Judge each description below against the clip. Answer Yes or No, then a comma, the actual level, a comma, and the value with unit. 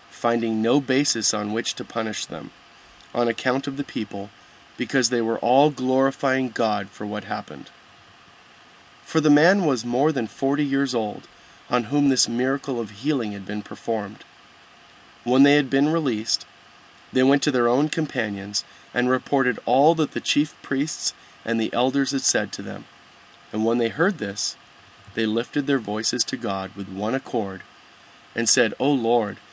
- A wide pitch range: No, average, 4.1 semitones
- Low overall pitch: Yes, low, 125 Hz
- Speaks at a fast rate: No, average, 170 wpm